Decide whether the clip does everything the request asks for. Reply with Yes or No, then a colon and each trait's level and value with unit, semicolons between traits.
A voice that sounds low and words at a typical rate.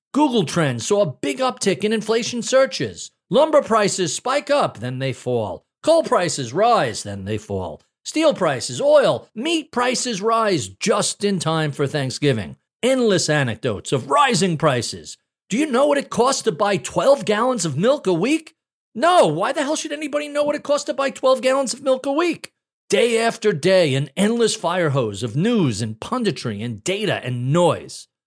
No: high, 210 Hz; average, 180 wpm